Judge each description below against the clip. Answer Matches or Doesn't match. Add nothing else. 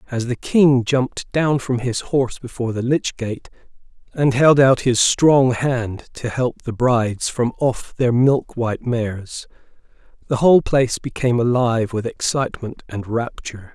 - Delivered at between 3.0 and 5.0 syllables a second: Matches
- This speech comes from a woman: Doesn't match